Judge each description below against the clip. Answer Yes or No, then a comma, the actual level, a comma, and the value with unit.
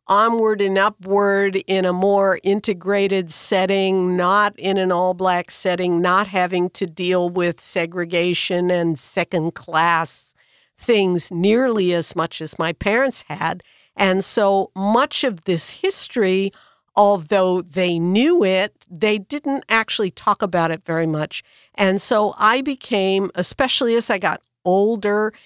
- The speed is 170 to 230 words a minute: No, slow, 135 wpm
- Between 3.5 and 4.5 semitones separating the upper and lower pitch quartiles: No, average, 2.8 semitones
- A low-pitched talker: No, high, 190 Hz